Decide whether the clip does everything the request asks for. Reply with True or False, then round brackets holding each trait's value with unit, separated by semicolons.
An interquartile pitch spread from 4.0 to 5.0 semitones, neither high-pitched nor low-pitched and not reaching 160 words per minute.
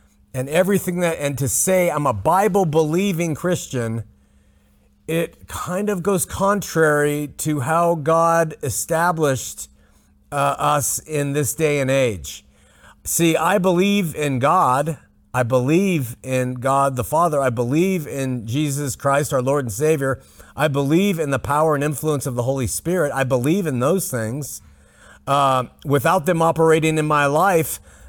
True (4.3 semitones; 150 Hz; 150 wpm)